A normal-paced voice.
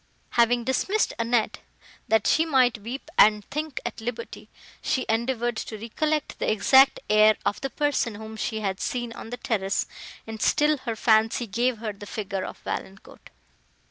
Yes: average, 165 wpm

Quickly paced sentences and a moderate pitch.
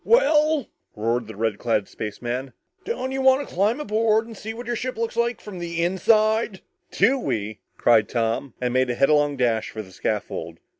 No: average, 180 wpm; medium, 175 Hz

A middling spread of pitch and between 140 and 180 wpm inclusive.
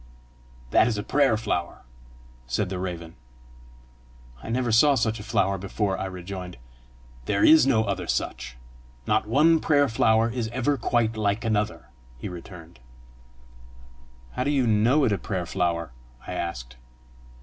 Yes: average, 4.7 semitones; average, 150 wpm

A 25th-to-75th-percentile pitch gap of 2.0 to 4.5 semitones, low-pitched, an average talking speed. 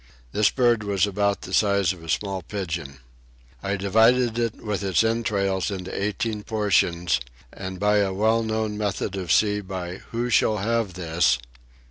Yes: average, 2.7 semitones; low, 100 Hz; average, 160 wpm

